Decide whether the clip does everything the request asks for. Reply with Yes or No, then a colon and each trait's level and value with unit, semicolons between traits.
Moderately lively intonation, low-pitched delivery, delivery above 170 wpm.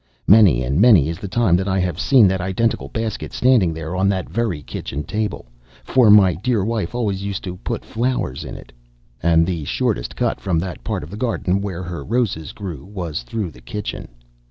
Yes: average, 4.5 semitones; very low, 95 Hz; fast, 205 wpm